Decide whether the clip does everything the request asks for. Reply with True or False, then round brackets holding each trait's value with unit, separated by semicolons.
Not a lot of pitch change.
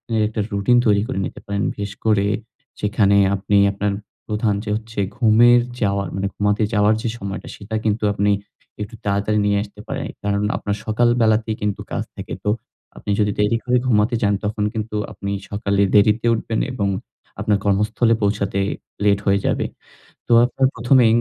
True (1.7 semitones)